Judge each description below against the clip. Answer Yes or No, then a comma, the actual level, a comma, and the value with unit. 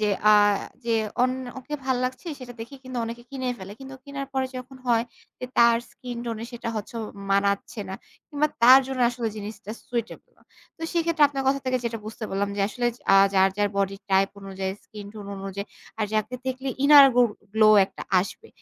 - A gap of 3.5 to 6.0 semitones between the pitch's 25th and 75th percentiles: Yes, average, 4.1 semitones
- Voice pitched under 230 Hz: No, high, 235 Hz